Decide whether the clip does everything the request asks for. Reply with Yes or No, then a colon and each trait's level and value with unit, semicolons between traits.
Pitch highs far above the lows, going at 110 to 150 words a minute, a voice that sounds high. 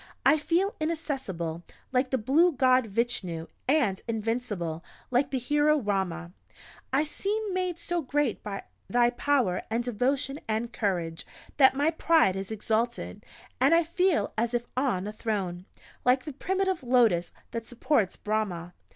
Yes: wide, 6.3 semitones; average, 145 wpm; high, 245 Hz